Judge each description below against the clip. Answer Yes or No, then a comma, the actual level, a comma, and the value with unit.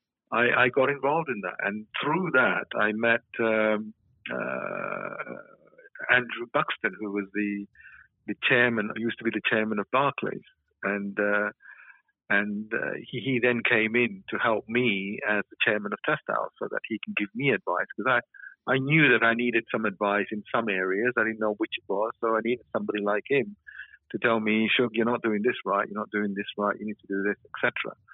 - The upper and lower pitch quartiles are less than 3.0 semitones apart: Yes, narrow, 2.6 semitones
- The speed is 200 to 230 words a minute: Yes, fast, 205 wpm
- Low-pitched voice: Yes, low, 110 Hz